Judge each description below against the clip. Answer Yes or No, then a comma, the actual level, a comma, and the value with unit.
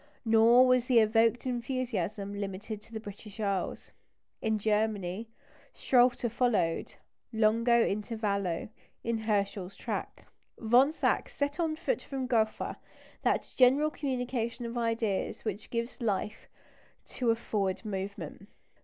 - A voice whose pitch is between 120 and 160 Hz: No, high, 225 Hz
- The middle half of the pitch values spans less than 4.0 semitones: Yes, average, 3.2 semitones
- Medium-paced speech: No, slow, 120 wpm